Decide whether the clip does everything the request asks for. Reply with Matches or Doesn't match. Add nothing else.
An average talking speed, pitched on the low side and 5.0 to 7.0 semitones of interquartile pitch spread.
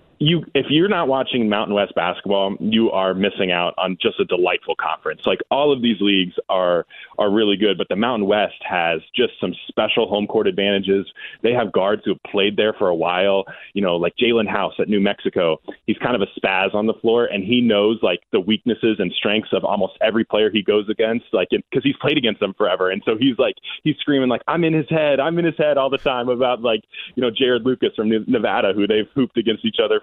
Doesn't match